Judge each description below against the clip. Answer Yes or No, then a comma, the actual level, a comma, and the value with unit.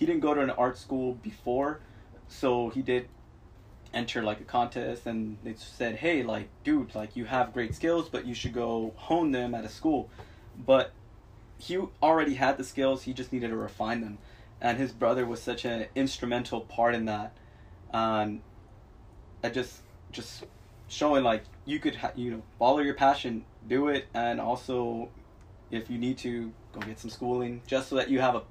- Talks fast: No, average, 185 wpm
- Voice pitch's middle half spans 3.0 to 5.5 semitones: No, narrow, 2.6 semitones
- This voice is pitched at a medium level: No, low, 120 Hz